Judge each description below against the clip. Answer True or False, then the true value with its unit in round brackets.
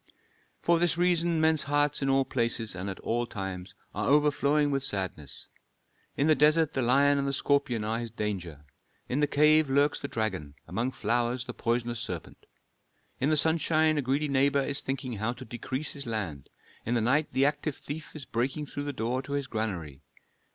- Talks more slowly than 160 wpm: False (190 wpm)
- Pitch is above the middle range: False (135 Hz)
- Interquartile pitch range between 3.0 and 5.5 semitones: True (4.3 semitones)